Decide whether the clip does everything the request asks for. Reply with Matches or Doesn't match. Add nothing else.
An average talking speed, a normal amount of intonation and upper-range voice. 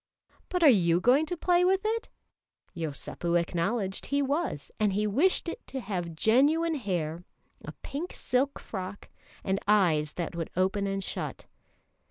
Doesn't match